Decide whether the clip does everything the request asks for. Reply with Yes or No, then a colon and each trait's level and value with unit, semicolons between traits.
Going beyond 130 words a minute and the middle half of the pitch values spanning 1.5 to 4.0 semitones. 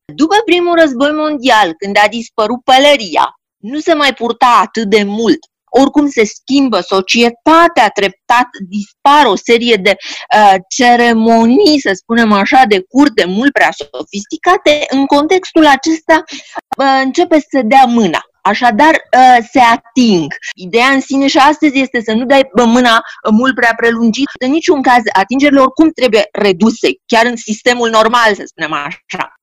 No: average, 150 wpm; average, 4.5 semitones